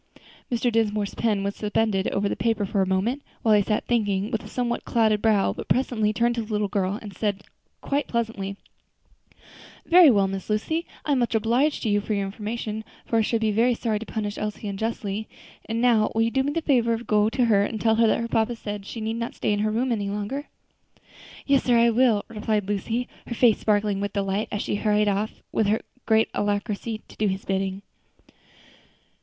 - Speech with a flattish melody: Yes, narrow, 2.3 semitones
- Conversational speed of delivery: No, fast, 215 wpm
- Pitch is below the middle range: No, high, 215 Hz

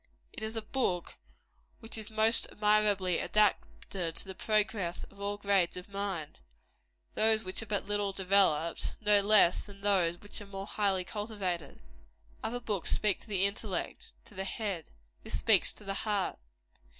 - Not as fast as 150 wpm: No, average, 160 wpm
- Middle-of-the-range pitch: No, high, 200 Hz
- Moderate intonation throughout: No, narrow, 2.2 semitones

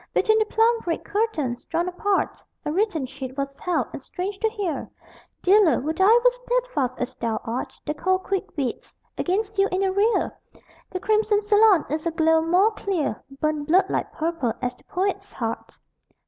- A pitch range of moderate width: No, wide, 5.7 semitones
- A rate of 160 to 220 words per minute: Yes, average, 180 wpm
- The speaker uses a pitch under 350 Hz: No, very high, 365 Hz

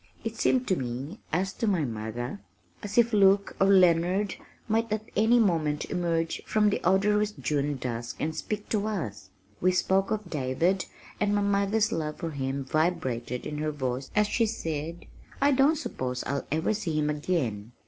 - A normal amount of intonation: No, wide, 6.4 semitones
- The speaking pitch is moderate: Yes, medium, 175 Hz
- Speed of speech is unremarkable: Yes, average, 175 wpm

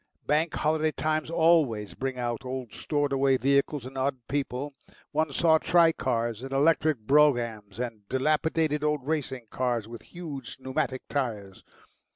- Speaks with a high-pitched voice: No, low, 135 Hz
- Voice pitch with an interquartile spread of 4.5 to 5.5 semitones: No, average, 3.8 semitones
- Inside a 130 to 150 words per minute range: Yes, average, 140 wpm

